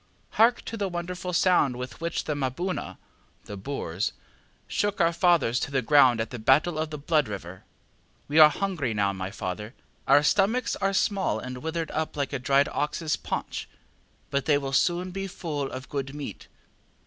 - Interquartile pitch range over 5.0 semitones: Yes, wide, 5.4 semitones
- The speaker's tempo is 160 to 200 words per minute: Yes, average, 180 wpm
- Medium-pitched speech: Yes, medium, 145 Hz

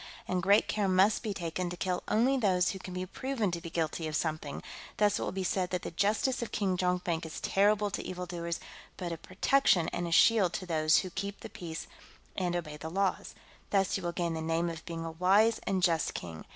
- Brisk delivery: Yes, fast, 230 wpm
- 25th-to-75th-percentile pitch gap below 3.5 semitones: Yes, average, 2.9 semitones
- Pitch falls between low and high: Yes, medium, 180 Hz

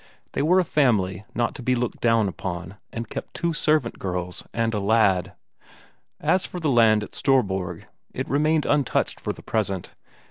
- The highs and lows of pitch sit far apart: Yes, wide, 6.6 semitones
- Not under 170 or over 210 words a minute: Yes, average, 175 wpm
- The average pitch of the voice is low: Yes, low, 115 Hz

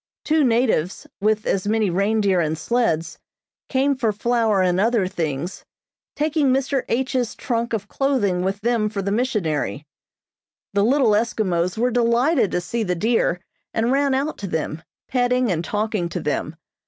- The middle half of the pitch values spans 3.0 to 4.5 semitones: No, average, 4.9 semitones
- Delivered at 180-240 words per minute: No, average, 155 wpm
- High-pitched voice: Yes, high, 220 Hz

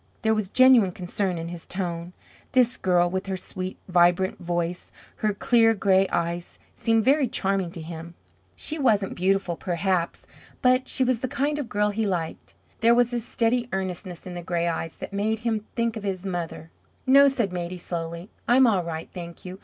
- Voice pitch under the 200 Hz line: Yes, high, 190 Hz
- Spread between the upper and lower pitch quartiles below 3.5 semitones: No, average, 4.6 semitones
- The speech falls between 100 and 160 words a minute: No, average, 185 wpm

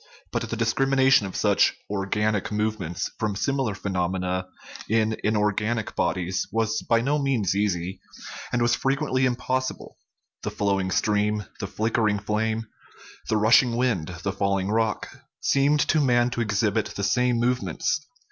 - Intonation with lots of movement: No, average, 3.4 semitones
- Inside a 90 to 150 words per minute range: Yes, average, 145 wpm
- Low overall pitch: Yes, low, 110 Hz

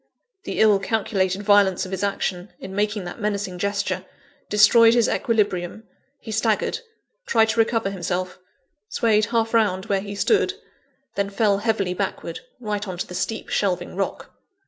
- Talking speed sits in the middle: Yes, average, 155 wpm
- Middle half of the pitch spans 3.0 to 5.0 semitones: No, narrow, 2.6 semitones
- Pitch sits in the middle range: No, high, 205 Hz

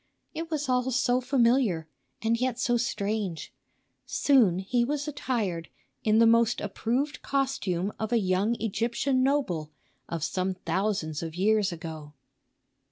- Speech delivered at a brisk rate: No, slow, 135 wpm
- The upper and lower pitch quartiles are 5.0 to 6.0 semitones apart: Yes, wide, 5.6 semitones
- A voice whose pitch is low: No, high, 225 Hz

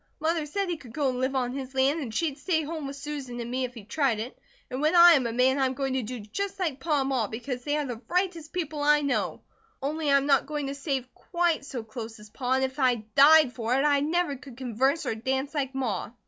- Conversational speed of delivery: No, fast, 265 wpm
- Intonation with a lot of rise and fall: No, average, 3.1 semitones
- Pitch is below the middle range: No, very high, 275 Hz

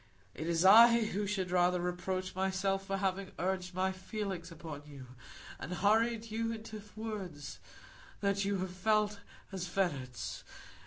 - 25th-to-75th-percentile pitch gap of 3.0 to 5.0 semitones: No, narrow, 2.6 semitones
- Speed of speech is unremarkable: Yes, average, 145 wpm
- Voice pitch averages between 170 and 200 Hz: Yes, high, 190 Hz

